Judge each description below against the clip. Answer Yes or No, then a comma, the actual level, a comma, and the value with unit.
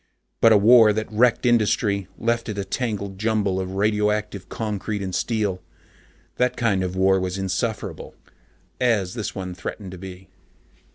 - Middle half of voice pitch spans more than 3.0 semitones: No, narrow, 2.6 semitones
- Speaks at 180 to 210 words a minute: No, average, 155 wpm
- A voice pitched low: Yes, low, 105 Hz